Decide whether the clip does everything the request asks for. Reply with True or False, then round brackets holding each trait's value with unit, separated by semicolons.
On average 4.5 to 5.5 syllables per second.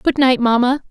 True (4.8 syllables/s)